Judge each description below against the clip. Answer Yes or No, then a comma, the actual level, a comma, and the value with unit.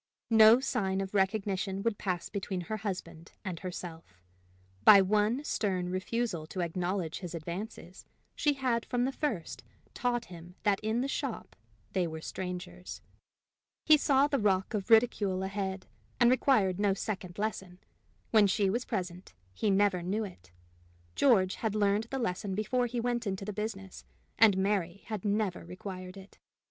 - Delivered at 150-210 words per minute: Yes, average, 155 wpm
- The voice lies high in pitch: Yes, high, 195 Hz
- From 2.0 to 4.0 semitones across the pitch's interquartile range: Yes, average, 3.3 semitones